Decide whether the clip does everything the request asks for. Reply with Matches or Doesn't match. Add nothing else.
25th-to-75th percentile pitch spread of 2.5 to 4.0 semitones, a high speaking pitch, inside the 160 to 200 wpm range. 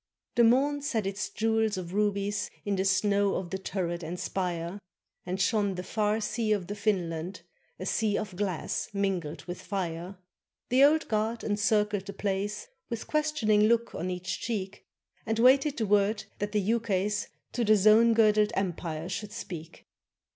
Matches